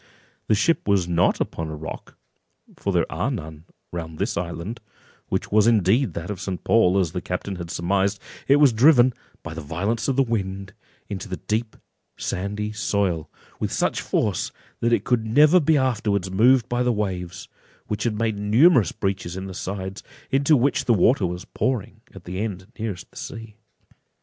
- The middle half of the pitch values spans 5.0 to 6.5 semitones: No, average, 4.4 semitones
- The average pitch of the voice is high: No, low, 100 Hz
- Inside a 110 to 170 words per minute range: No, average, 185 wpm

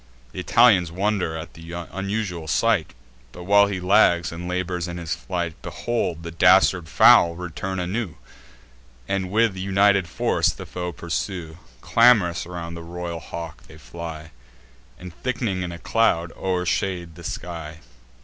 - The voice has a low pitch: Yes, very low, 90 Hz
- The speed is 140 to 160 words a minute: Yes, average, 145 wpm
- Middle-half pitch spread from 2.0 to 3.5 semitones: Yes, narrow, 2.4 semitones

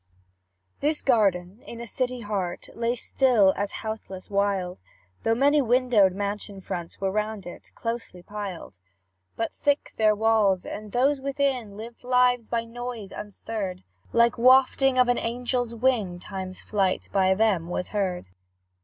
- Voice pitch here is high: Yes, high, 220 Hz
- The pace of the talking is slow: No, average, 145 wpm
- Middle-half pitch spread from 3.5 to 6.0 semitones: Yes, average, 4.1 semitones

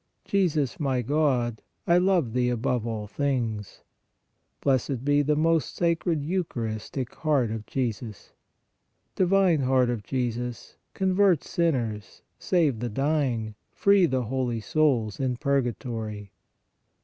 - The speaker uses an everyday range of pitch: Yes, average, 5.0 semitones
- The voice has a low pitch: Yes, low, 130 Hz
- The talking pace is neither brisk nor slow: No, slow, 115 wpm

